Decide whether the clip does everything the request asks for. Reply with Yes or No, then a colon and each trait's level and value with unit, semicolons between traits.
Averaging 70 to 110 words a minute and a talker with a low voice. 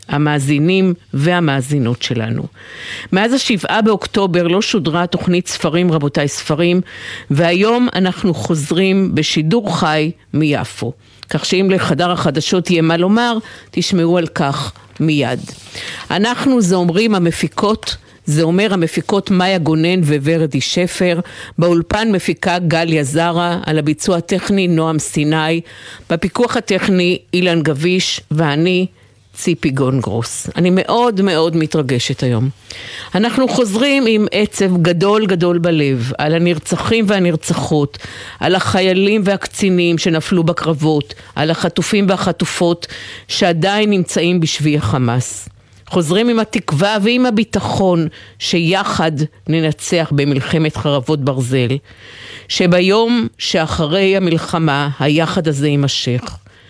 No: average, 105 wpm; medium, 170 Hz